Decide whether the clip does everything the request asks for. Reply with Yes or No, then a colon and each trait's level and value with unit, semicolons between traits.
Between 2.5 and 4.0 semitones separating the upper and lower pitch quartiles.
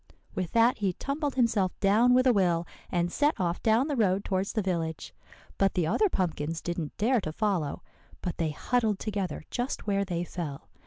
No: average, 5.1 semitones